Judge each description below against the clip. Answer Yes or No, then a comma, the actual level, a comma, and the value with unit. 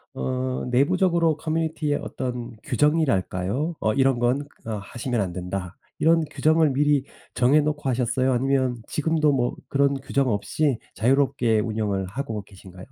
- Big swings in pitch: No, average, 4.7 semitones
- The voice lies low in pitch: Yes, low, 130 Hz